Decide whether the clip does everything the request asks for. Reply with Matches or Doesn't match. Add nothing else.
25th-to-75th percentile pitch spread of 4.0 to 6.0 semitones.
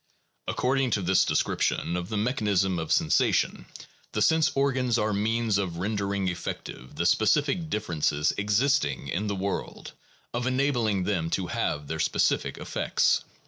Matches